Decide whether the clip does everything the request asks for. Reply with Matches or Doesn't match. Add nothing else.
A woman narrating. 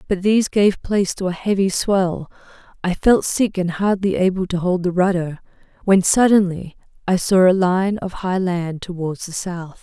Matches